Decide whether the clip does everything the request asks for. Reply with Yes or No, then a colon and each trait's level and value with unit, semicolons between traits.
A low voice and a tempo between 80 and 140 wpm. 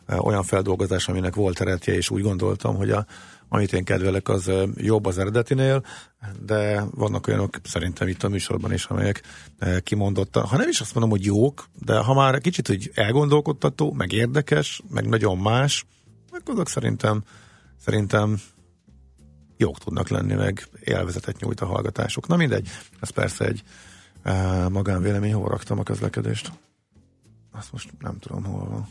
No: low, 105 Hz; average, 150 wpm